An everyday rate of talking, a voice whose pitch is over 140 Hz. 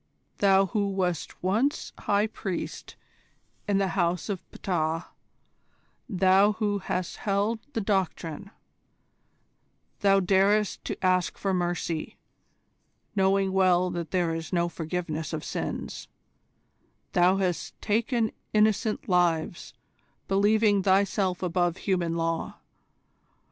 No: slow, 105 wpm; high, 190 Hz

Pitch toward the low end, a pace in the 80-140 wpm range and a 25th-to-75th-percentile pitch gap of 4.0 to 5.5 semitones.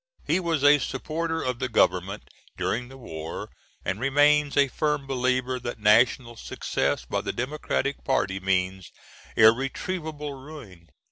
Yes: low, 130 Hz; slow, 135 wpm; average, 5.1 semitones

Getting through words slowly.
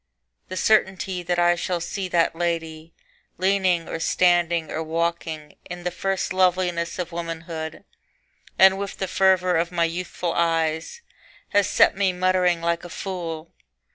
No: average, 145 wpm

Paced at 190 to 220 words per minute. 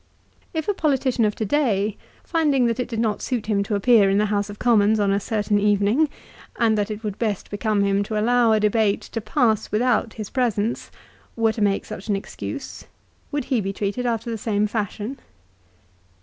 Yes: average, 200 wpm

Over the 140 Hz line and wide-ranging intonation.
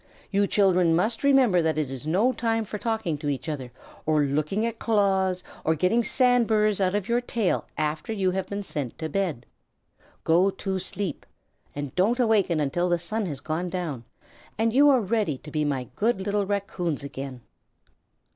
Yes: medium, 185 Hz; wide, 5.7 semitones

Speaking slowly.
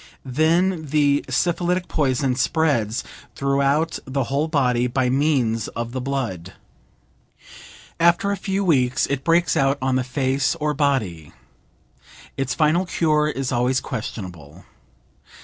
Yes: slow, 125 wpm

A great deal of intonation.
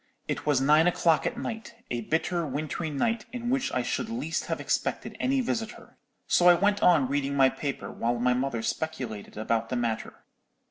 Yes: wide, 8.3 semitones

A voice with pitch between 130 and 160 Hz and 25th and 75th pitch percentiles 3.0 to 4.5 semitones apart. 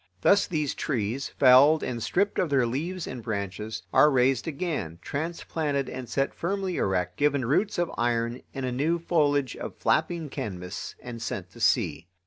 No: low, 135 Hz; wide, 5.6 semitones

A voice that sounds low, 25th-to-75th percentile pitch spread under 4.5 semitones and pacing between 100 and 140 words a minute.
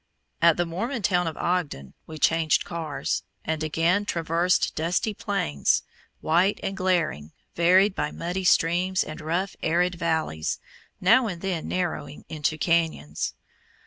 No: medium, 170 Hz; narrow, 2.6 semitones; slow, 135 wpm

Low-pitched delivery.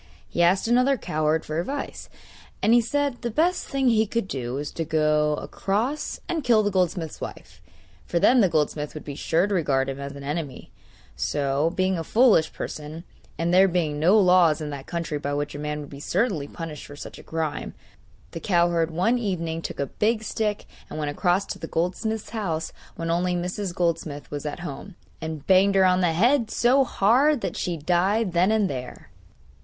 No: medium, 175 Hz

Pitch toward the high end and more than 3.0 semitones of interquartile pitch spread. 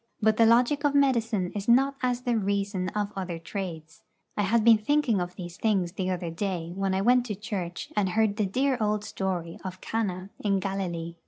Yes: high, 200 Hz; average, 3.7 semitones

